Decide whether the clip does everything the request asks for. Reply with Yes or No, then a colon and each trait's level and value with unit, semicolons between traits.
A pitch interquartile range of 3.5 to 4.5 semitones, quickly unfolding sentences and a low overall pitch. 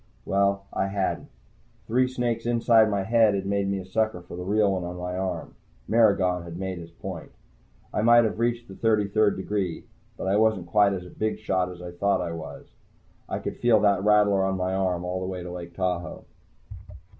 No: average, 3.0 semitones; fast, 210 wpm; very low, 95 Hz